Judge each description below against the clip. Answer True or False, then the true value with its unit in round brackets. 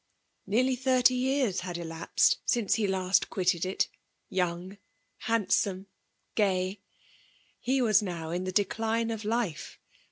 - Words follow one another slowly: True (125 wpm)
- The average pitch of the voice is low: False (200 Hz)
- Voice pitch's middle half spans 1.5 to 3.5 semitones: False (3.9 semitones)